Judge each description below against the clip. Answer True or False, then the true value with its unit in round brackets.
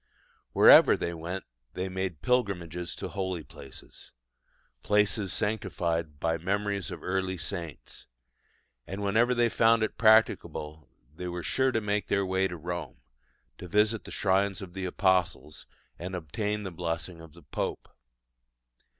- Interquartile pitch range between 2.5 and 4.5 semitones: True (3.2 semitones)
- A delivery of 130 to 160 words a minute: True (140 wpm)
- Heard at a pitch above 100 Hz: False (95 Hz)